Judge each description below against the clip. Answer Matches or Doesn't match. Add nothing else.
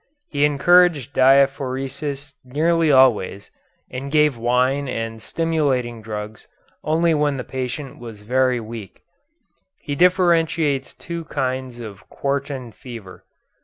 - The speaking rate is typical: Doesn't match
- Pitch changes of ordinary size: Matches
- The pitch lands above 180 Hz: Doesn't match